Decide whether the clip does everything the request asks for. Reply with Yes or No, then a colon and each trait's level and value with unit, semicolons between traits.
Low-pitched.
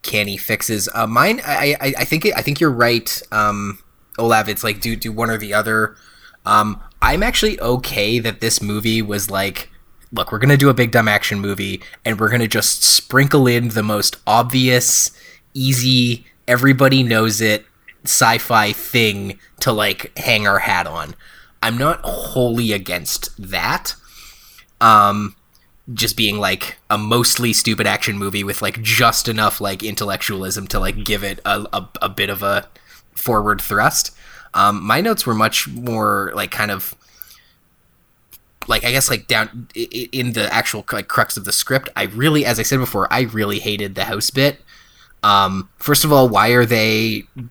Yes: low, 110 Hz